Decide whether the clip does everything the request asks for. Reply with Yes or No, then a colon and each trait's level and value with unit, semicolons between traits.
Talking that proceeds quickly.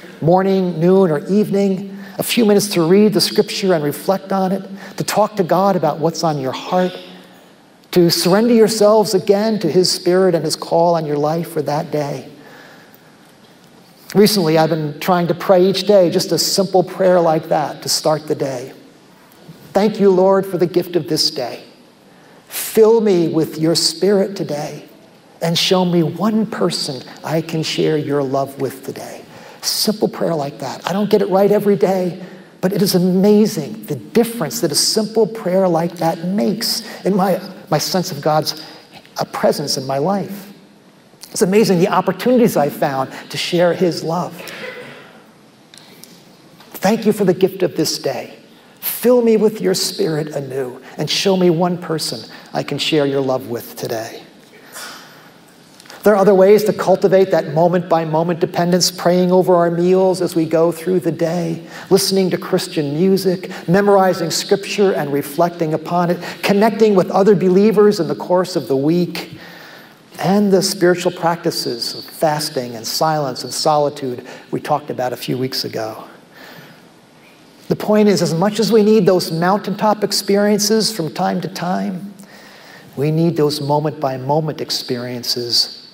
No: average, 165 wpm